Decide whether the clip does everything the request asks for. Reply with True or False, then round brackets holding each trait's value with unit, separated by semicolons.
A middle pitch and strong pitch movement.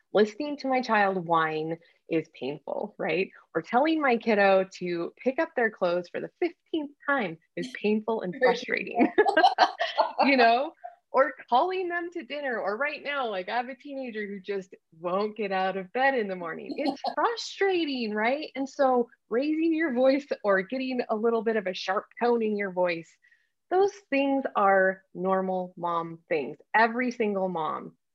False (240 Hz; 6.9 semitones)